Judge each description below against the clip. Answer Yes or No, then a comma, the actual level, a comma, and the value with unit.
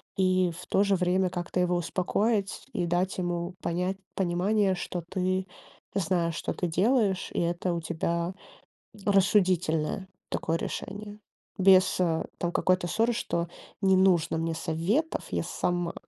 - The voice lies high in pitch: No, medium, 180 Hz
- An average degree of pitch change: No, narrow, 2.0 semitones